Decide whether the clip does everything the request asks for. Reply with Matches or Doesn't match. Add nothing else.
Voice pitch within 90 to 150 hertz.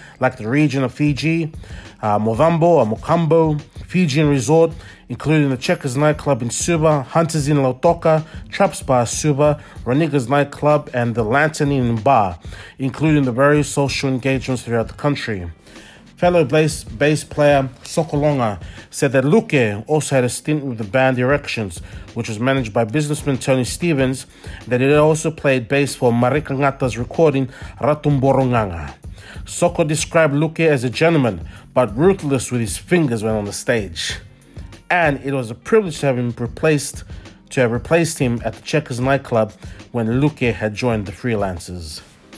Matches